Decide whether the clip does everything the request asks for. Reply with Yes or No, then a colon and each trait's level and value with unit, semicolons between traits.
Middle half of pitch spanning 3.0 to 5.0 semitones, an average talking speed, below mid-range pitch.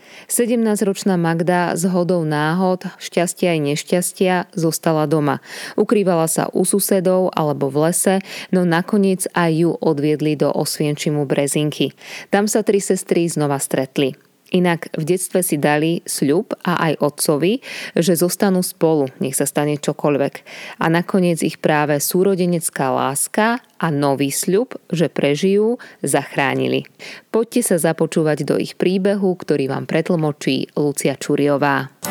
No: average, 4.0 semitones; average, 130 wpm; medium, 170 Hz